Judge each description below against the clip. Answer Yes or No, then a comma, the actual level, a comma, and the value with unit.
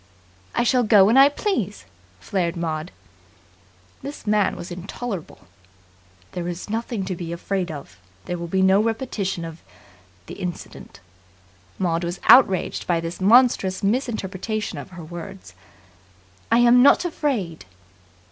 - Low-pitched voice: No, high, 190 Hz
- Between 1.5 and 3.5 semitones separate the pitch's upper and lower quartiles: No, average, 4.8 semitones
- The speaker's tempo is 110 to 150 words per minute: Yes, slow, 135 wpm